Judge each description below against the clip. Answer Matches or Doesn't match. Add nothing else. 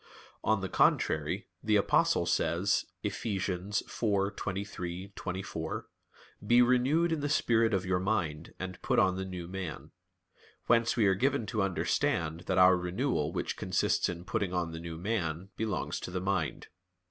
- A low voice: Matches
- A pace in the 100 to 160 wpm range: Matches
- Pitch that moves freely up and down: Doesn't match